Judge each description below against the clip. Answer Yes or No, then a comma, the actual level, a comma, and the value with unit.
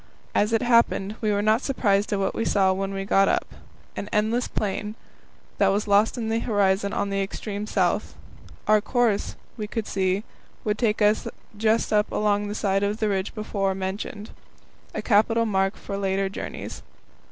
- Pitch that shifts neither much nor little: No, narrow, 1.8 semitones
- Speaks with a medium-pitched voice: No, high, 205 Hz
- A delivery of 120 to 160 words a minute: No, average, 175 wpm